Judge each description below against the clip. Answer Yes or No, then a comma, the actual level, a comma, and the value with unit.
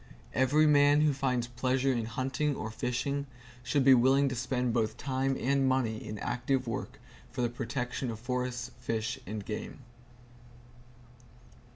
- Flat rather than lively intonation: Yes, narrow, 2.2 semitones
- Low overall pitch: Yes, low, 125 Hz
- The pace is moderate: Yes, average, 150 wpm